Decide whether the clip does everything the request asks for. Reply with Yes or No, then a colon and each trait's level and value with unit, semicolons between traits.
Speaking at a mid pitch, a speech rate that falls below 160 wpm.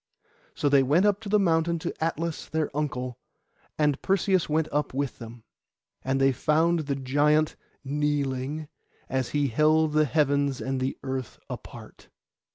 Yes: medium, 150 Hz; average, 150 wpm